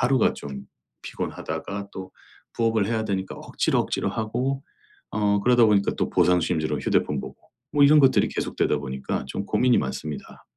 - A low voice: Yes, low, 105 Hz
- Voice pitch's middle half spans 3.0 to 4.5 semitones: No, average, 5.3 semitones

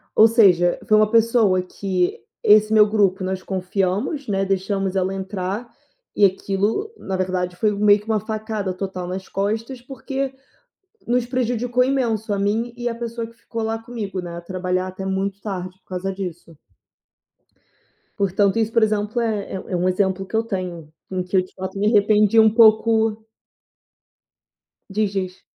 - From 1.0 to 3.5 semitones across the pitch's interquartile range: Yes, average, 3.1 semitones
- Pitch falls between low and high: No, high, 205 Hz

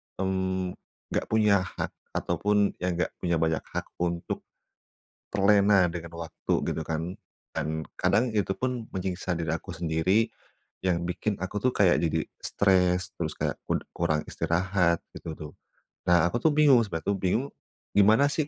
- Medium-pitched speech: No, very low, 90 Hz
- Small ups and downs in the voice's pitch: No, average, 3.2 semitones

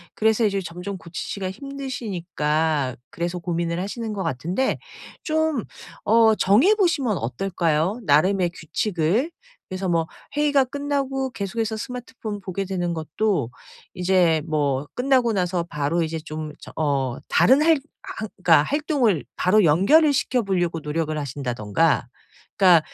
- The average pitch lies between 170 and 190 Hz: Yes, medium, 185 Hz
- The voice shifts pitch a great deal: Yes, wide, 6.3 semitones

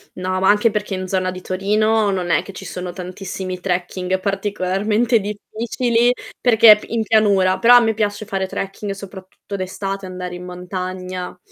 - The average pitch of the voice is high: Yes, high, 195 Hz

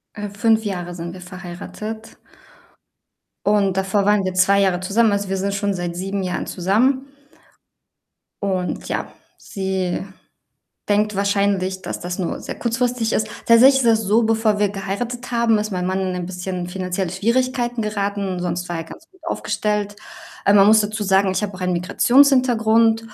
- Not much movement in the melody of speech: No, average, 3.0 semitones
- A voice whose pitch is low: No, high, 200 Hz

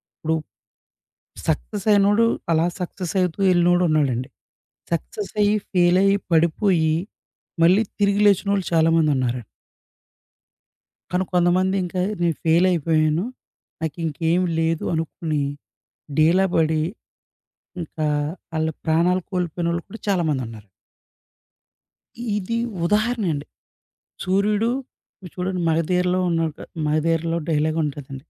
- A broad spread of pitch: No, average, 2.8 semitones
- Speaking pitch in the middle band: Yes, medium, 170 Hz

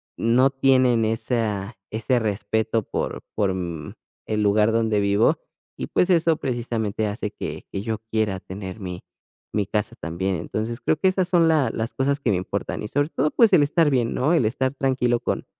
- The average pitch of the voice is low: Yes, low, 115 Hz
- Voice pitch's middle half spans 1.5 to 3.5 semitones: No, average, 4.2 semitones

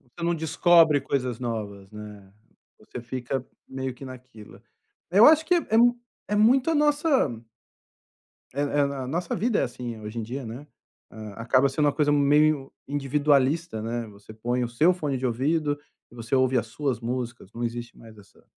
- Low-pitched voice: Yes, low, 130 Hz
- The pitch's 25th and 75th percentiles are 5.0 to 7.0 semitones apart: No, average, 4.6 semitones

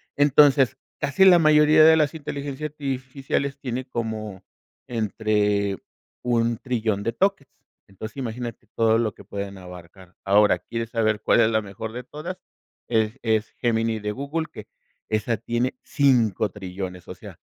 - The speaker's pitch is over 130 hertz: No, low, 115 Hz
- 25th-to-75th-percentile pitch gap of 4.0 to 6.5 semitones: Yes, average, 4.7 semitones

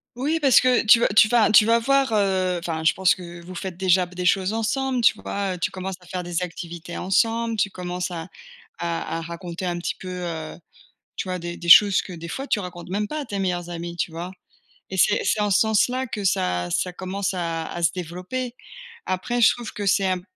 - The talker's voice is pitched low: No, medium, 185 Hz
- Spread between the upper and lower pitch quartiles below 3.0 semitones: No, average, 3.5 semitones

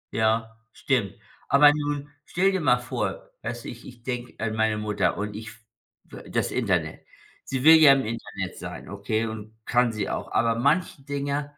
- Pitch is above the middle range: No, low, 120 Hz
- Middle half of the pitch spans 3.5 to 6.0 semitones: Yes, average, 4.4 semitones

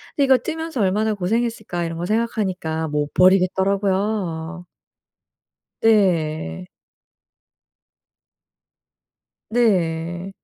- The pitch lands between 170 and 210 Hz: Yes, high, 190 Hz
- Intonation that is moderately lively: Yes, average, 4.7 semitones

